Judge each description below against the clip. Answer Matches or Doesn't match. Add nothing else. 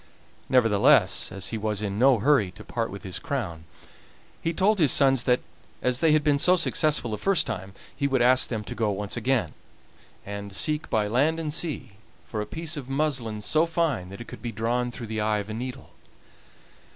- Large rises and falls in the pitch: Matches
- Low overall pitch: Matches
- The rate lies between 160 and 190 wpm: Doesn't match